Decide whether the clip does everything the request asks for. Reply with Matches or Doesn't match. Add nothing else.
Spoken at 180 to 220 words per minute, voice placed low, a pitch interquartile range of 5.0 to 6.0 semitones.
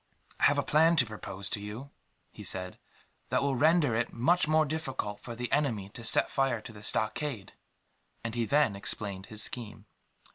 Matches